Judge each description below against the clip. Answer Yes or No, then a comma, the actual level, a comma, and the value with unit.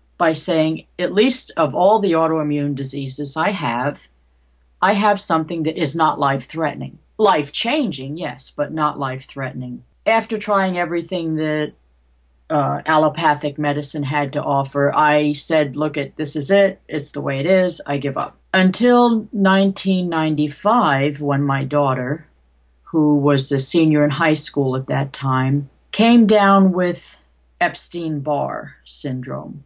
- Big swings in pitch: No, average, 4.0 semitones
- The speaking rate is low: No, average, 145 wpm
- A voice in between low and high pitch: Yes, medium, 150 Hz